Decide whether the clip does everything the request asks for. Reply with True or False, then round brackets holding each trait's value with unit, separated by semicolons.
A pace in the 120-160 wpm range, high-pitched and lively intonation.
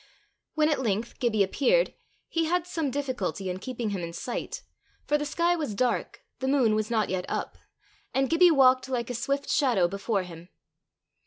False (180 wpm; 255 Hz; 6.4 semitones)